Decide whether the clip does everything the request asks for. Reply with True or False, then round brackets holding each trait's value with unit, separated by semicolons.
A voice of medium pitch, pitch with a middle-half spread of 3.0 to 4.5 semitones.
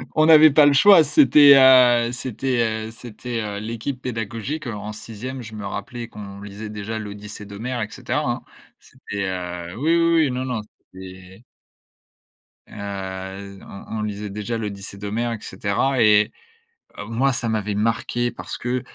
False (110 Hz; 3.7 semitones)